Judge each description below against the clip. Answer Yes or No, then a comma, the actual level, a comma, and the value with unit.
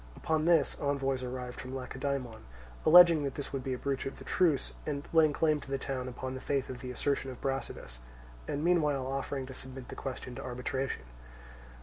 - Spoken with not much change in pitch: Yes, narrow, 2.0 semitones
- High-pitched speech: No, low, 135 Hz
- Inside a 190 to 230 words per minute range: Yes, average, 200 wpm